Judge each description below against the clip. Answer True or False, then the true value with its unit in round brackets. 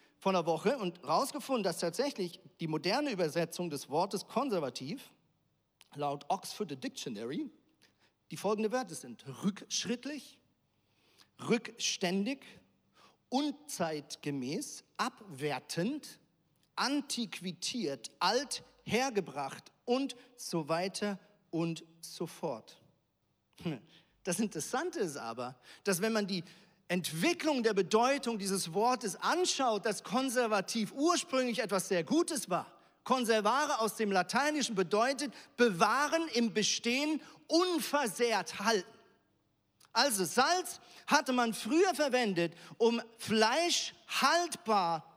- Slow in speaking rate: True (95 wpm)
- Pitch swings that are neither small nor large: False (6.7 semitones)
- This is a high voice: True (220 Hz)